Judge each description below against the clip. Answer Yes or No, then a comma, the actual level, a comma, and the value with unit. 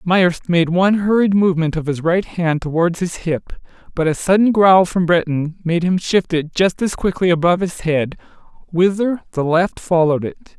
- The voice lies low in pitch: No, medium, 175 Hz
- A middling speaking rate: Yes, average, 185 wpm